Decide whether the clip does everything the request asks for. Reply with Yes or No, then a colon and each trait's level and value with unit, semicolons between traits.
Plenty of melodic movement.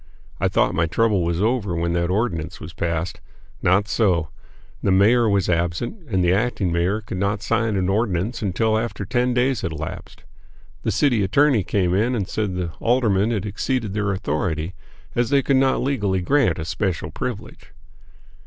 No: average, 4.8 semitones